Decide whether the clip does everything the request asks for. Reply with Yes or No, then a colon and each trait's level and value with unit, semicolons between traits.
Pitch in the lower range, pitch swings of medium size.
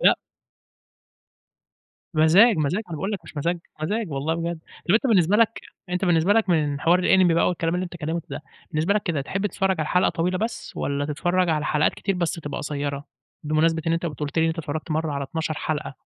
No: medium, 165 Hz; average, 3.1 semitones